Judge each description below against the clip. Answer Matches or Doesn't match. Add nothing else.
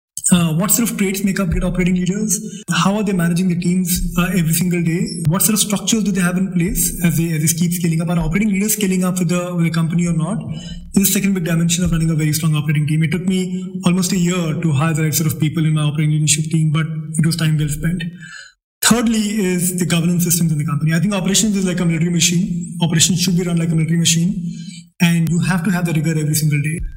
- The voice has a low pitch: Doesn't match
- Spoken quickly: Matches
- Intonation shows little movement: Matches